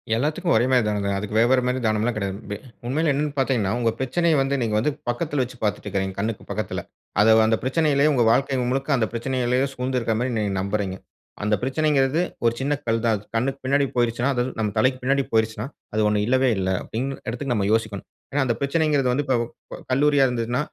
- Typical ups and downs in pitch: Yes, average, 3.6 semitones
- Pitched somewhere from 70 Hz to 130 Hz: Yes, low, 125 Hz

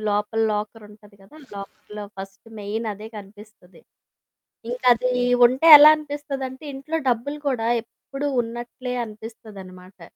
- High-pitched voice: Yes, high, 225 Hz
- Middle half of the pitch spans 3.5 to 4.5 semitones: Yes, average, 3.9 semitones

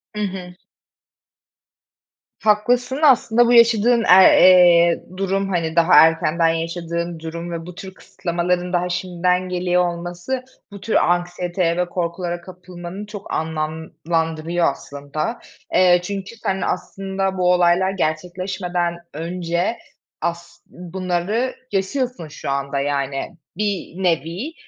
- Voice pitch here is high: No, medium, 180 Hz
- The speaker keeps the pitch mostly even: Yes, narrow, 2.2 semitones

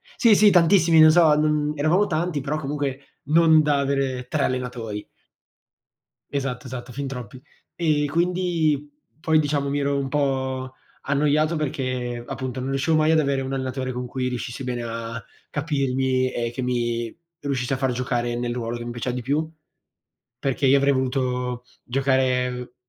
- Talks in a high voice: No, low, 135 Hz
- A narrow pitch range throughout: No, average, 3.0 semitones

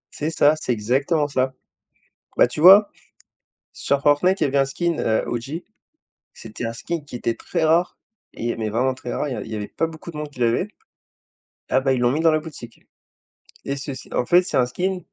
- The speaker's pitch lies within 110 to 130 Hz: No, medium, 140 Hz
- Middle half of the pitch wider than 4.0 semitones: Yes, average, 4.8 semitones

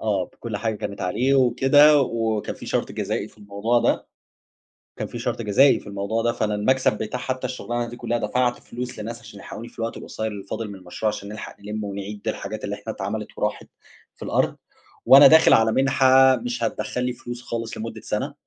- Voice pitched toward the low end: Yes, low, 115 Hz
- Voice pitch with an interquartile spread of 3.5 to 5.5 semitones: No, average, 2.9 semitones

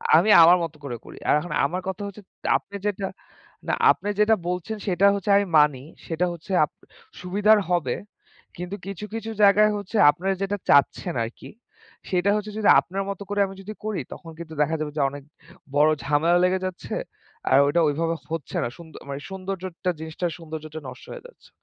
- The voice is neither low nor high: Yes, medium, 180 Hz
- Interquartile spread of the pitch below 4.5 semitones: Yes, average, 4.0 semitones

